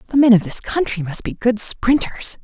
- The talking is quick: Yes, fast, 220 wpm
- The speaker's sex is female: Yes, female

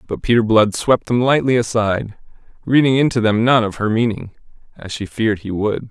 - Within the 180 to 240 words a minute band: Yes, average, 195 wpm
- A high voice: No, low, 115 Hz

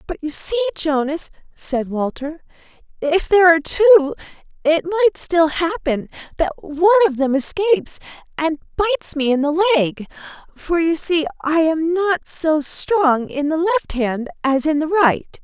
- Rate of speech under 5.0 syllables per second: Yes, 4.8 syllables/s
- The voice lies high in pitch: Yes, very high, 325 Hz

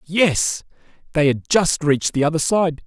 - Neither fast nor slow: Yes, average, 170 wpm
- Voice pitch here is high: No, medium, 160 Hz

